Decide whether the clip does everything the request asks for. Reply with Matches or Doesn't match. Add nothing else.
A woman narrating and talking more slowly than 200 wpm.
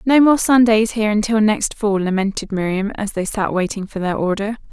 Doesn't match